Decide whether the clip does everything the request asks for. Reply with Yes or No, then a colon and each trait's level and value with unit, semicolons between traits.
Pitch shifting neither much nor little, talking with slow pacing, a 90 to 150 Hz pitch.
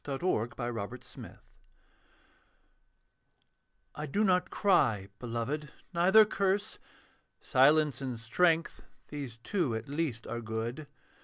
No: wide, 6.5 semitones; slow, 100 wpm; medium, 140 Hz